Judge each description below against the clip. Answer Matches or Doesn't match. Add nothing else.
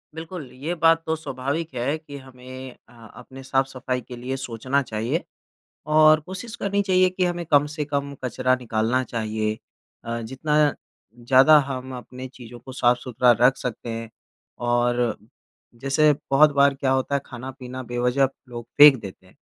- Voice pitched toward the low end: Matches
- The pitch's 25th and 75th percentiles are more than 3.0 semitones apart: Matches